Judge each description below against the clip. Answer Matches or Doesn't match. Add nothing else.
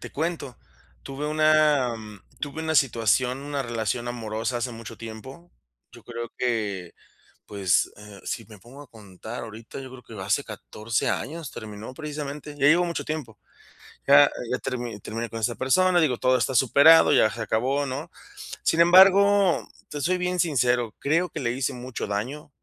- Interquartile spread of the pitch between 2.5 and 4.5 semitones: Doesn't match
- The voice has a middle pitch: Doesn't match